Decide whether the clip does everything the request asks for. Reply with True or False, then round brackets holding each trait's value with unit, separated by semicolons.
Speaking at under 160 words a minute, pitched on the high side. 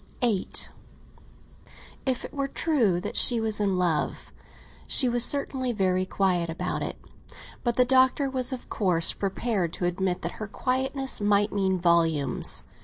True (150 wpm; 205 Hz)